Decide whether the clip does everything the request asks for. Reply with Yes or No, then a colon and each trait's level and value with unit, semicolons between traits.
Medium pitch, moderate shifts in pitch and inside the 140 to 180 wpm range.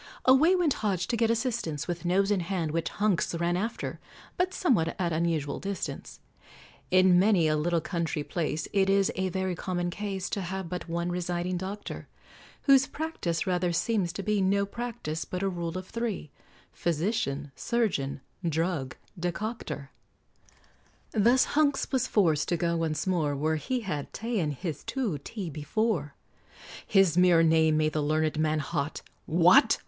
Yes: medium, 180 Hz; average, 4.4 semitones; average, 160 wpm